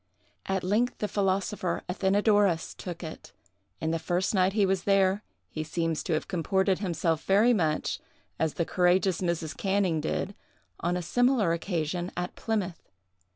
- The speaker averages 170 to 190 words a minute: No, average, 155 wpm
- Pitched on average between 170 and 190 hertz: Yes, medium, 185 Hz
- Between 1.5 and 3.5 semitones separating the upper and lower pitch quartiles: Yes, average, 3.0 semitones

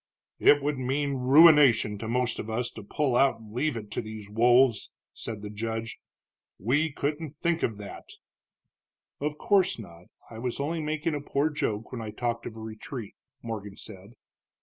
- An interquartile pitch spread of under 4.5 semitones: No, average, 4.9 semitones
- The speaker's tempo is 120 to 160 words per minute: No, average, 175 wpm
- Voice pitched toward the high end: No, low, 120 Hz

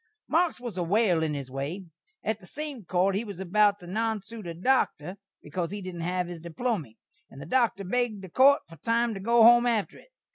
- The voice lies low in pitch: No, high, 200 Hz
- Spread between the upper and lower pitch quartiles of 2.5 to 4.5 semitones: No, average, 5.1 semitones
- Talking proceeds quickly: Yes, fast, 215 wpm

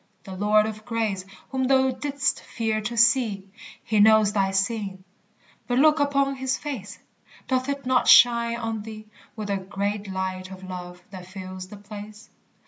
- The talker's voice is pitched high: Yes, high, 215 Hz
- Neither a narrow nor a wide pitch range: Yes, average, 4.0 semitones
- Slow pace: No, average, 165 wpm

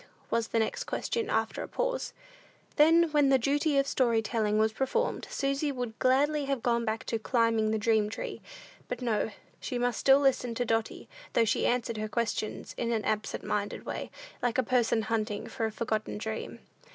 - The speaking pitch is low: No, high, 235 Hz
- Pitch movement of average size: Yes, average, 3.5 semitones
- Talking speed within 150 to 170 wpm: No, average, 190 wpm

